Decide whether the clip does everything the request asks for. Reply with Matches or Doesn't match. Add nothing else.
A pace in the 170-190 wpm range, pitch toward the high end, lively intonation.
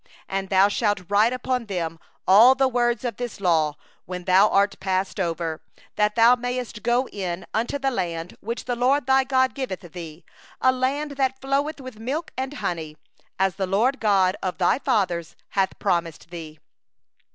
Matches